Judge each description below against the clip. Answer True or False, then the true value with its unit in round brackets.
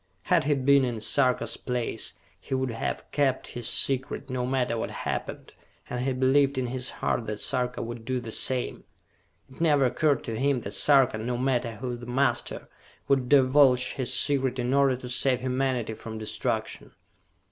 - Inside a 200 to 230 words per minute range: False (175 wpm)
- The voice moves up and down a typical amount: False (1.8 semitones)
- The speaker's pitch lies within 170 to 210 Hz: False (130 Hz)